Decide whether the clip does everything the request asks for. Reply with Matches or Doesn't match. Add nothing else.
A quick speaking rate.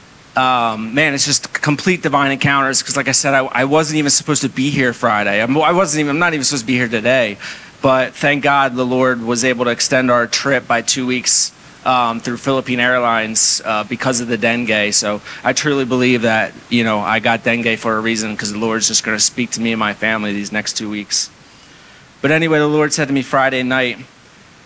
Matches